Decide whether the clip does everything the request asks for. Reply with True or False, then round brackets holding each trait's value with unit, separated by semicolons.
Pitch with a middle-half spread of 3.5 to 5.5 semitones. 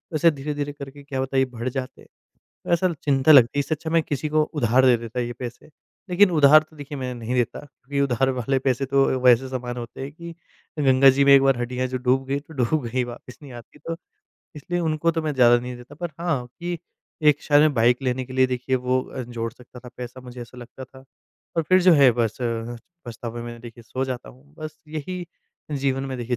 False (3.0 semitones)